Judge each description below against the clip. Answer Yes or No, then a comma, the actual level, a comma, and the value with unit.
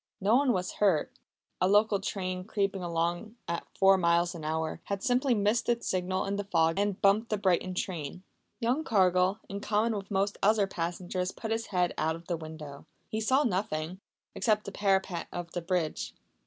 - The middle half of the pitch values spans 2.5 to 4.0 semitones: Yes, average, 3.2 semitones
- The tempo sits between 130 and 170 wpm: No, average, 185 wpm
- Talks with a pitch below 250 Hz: Yes, high, 190 Hz